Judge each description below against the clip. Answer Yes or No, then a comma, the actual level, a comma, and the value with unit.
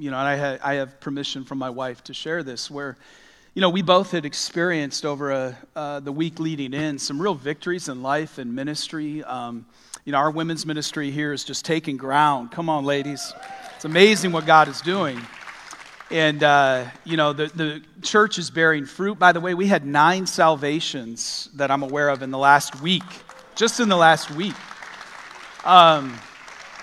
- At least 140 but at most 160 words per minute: No, average, 190 wpm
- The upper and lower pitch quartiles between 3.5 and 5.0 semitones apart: No, average, 3.0 semitones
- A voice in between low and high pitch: Yes, medium, 150 Hz